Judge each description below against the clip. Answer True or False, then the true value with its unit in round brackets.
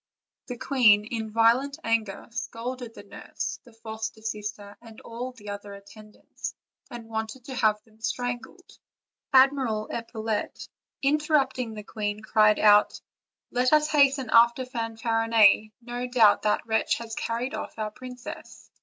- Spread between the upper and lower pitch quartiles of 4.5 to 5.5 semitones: False (2.6 semitones)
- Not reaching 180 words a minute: True (140 wpm)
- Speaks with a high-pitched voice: True (230 Hz)